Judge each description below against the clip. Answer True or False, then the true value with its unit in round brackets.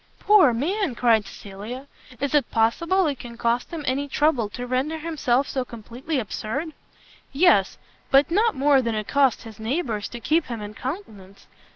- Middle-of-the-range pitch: False (260 Hz)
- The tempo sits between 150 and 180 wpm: True (170 wpm)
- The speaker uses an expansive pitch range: False (5.0 semitones)